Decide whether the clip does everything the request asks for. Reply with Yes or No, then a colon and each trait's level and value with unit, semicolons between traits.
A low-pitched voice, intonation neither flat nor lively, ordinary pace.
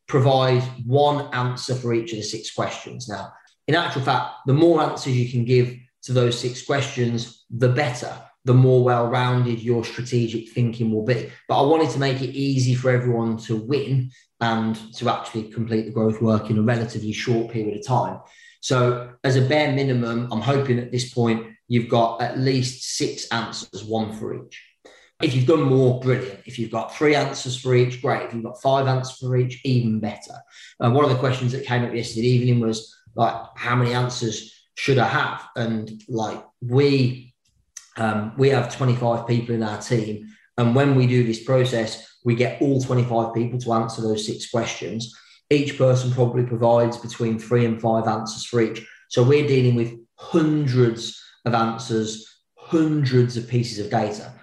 No: low, 120 Hz; narrow, 2.1 semitones; average, 185 wpm